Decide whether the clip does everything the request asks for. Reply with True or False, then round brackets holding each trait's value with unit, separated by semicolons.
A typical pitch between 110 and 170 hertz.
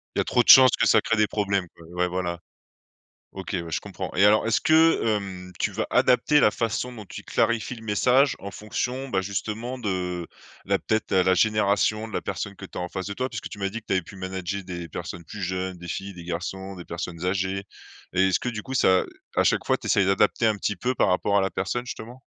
False (100 Hz)